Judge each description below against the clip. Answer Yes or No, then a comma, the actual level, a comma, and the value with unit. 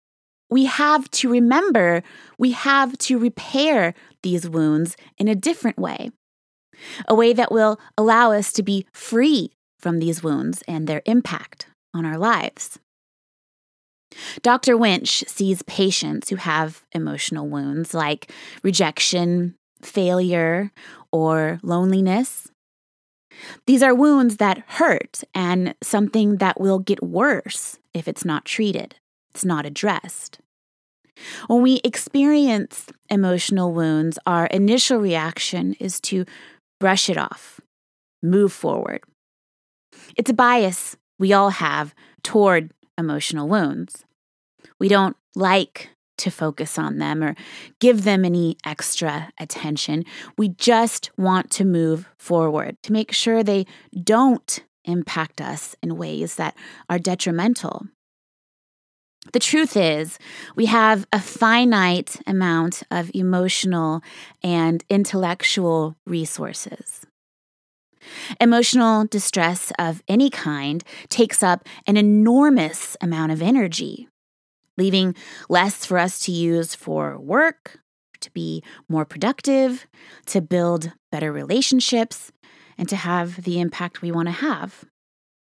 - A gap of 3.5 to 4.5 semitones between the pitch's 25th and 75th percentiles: No, wide, 5.5 semitones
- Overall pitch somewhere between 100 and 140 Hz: No, high, 190 Hz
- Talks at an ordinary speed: No, slow, 120 wpm